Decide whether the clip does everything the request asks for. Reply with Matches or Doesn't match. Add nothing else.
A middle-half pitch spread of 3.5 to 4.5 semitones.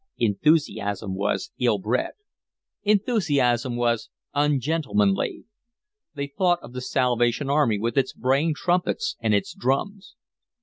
Doesn't match